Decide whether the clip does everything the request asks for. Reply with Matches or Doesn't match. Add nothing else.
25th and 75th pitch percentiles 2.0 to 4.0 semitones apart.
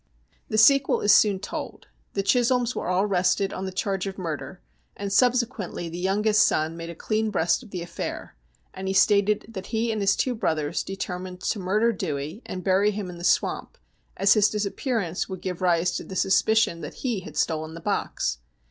Matches